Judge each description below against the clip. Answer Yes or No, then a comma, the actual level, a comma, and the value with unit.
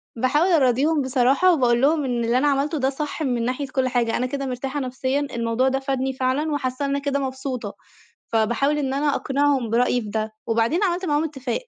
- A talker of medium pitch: No, very high, 265 Hz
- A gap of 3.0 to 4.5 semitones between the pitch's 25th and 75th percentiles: No, narrow, 2.6 semitones